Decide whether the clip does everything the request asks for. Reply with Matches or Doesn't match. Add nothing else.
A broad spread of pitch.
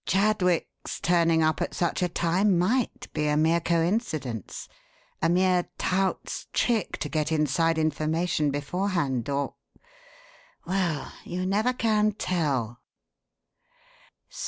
Doesn't match